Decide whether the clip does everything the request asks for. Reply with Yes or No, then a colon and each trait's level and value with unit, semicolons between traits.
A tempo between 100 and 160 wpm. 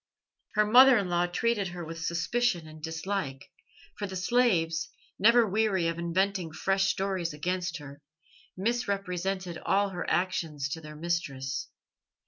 Yes: slow, 135 wpm